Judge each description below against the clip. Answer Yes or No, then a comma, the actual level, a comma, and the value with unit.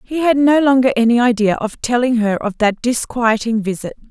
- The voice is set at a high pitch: Yes, high, 240 Hz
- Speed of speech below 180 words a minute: No, average, 190 wpm